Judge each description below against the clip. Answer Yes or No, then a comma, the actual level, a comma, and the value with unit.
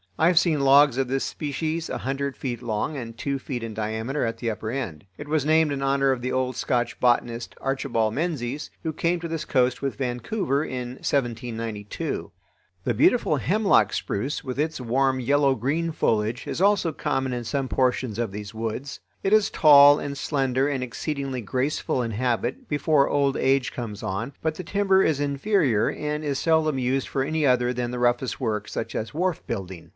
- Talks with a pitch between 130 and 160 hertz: Yes, low, 135 Hz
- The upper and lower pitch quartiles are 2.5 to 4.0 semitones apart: Yes, average, 3.7 semitones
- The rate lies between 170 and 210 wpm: Yes, average, 190 wpm